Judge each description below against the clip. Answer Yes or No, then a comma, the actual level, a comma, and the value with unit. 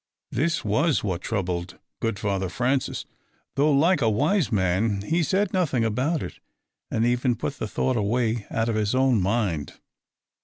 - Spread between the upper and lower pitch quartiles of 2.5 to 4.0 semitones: No, average, 5.3 semitones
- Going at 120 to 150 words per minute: No, average, 165 wpm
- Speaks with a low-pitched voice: Yes, low, 115 Hz